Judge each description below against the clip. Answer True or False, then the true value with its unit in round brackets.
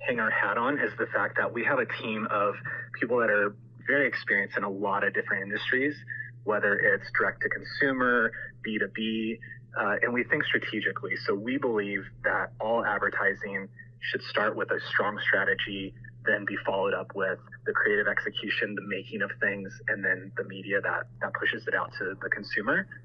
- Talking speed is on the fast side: False (185 wpm)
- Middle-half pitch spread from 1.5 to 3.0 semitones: True (2.5 semitones)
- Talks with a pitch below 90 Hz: False (120 Hz)